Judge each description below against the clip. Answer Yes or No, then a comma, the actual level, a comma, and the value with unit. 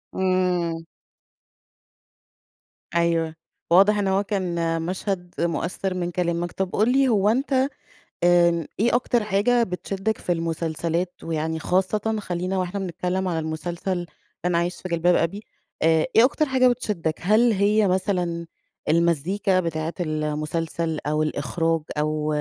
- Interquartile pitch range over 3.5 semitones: No, average, 3.1 semitones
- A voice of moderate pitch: Yes, medium, 175 Hz